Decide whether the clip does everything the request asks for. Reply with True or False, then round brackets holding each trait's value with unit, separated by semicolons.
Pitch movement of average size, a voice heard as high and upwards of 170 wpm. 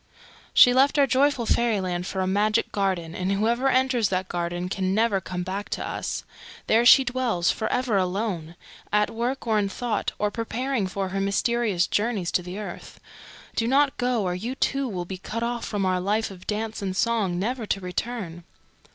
True (4.3 semitones; 210 Hz; 190 wpm)